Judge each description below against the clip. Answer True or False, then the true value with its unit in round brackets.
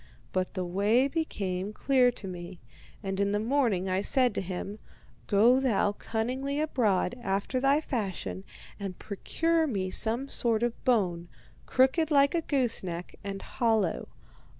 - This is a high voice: True (220 Hz)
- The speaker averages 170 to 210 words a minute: False (150 wpm)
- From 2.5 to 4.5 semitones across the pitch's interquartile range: False (5.4 semitones)